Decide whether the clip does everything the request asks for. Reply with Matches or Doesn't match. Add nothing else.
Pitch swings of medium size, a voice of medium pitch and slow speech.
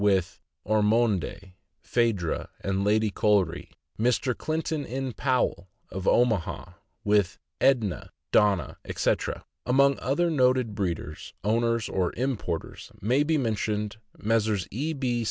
Doesn't match